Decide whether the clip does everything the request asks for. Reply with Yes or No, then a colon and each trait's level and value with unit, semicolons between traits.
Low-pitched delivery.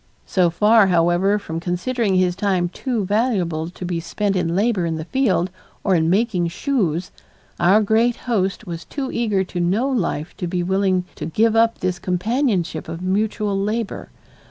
No: high, 190 Hz